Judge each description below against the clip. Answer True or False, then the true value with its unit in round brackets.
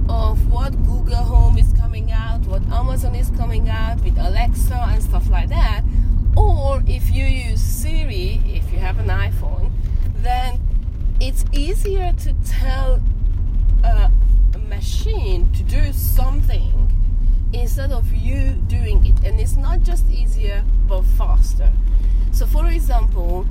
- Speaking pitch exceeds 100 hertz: False (85 Hz)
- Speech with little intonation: True (1.4 semitones)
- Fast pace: False (135 wpm)